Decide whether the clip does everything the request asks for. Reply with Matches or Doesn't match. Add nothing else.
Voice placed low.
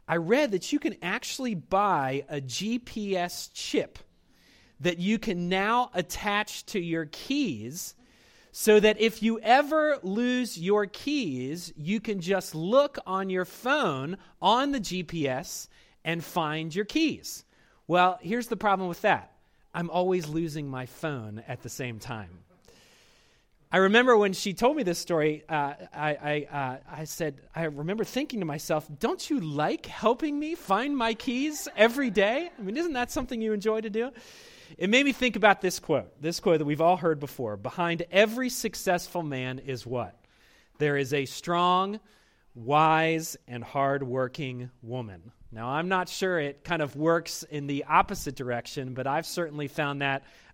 Doesn't match